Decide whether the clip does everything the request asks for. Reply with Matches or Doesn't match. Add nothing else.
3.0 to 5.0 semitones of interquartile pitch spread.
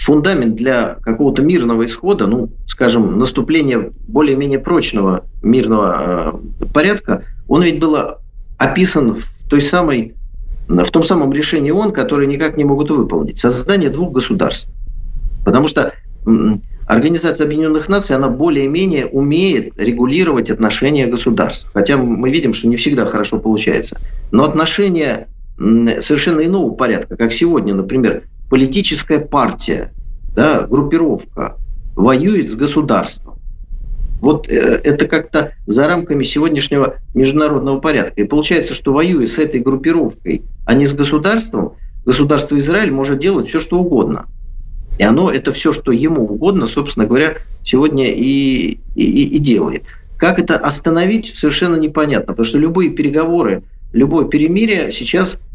Matches